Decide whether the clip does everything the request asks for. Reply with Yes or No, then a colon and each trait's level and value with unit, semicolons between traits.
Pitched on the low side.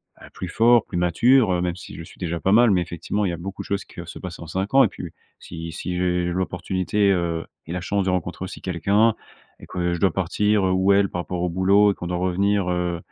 Yes: very low, 90 Hz